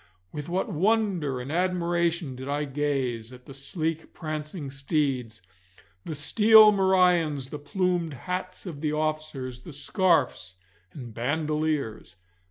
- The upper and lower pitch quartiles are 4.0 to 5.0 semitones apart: Yes, average, 4.4 semitones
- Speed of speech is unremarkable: No, slow, 125 wpm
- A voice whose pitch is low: No, medium, 150 Hz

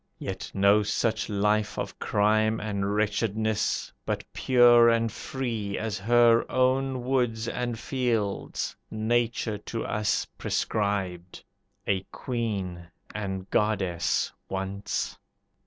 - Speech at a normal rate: No, slow, 105 wpm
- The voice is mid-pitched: No, low, 110 Hz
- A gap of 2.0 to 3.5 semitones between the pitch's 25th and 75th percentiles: Yes, average, 2.8 semitones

